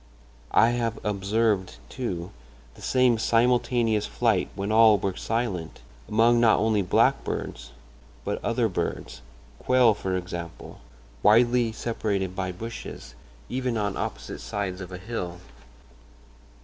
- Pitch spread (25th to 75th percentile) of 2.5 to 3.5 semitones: No, average, 4.0 semitones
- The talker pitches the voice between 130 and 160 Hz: No, low, 105 Hz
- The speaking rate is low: Yes, slow, 110 wpm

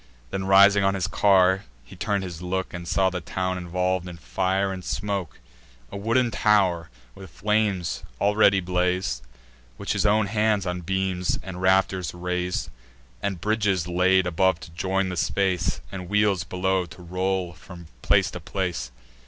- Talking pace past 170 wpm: No, average, 160 wpm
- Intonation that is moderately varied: No, narrow, 1.6 semitones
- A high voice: No, very low, 95 Hz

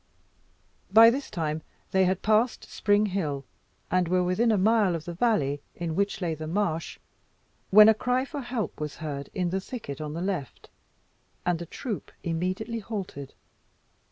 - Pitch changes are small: No, average, 5.0 semitones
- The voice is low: No, medium, 185 Hz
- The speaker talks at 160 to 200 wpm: Yes, average, 165 wpm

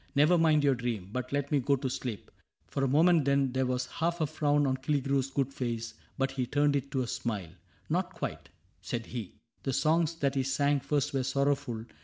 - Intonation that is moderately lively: No, narrow, 2.2 semitones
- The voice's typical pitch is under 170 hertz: Yes, low, 135 Hz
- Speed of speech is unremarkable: No, fast, 230 wpm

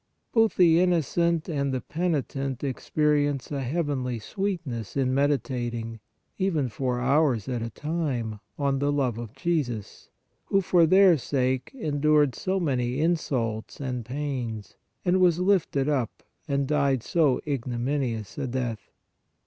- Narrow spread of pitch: No, average, 4.3 semitones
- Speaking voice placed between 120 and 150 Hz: Yes, medium, 140 Hz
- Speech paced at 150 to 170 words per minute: No, average, 140 wpm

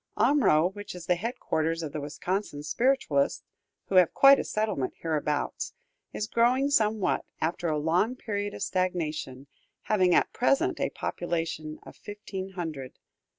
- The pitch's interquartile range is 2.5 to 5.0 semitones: No, wide, 5.4 semitones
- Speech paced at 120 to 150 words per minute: Yes, average, 145 wpm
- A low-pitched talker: No, medium, 180 Hz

